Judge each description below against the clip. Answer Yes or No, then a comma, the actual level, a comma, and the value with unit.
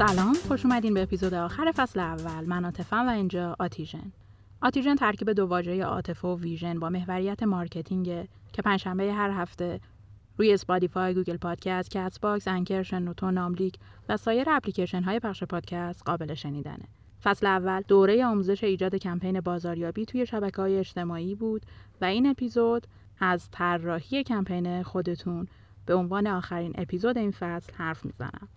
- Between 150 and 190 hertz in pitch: Yes, medium, 185 Hz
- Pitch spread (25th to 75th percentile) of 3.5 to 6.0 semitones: No, average, 2.7 semitones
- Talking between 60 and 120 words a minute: No, average, 145 wpm